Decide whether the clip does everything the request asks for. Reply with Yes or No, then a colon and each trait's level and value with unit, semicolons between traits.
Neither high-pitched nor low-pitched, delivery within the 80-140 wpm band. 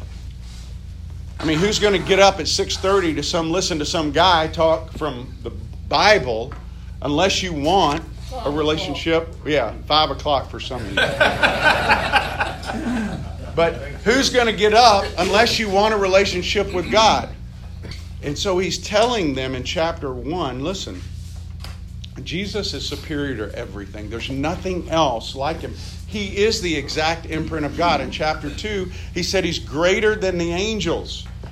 No: medium, 155 Hz; average, 150 wpm